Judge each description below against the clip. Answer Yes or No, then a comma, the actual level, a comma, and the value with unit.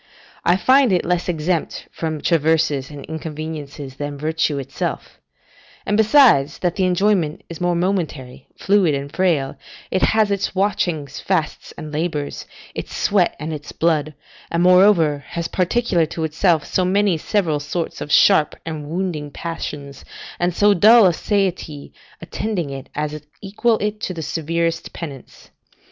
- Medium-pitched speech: Yes, medium, 165 Hz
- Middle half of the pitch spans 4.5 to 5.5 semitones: No, average, 3.9 semitones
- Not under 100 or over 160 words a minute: Yes, average, 150 wpm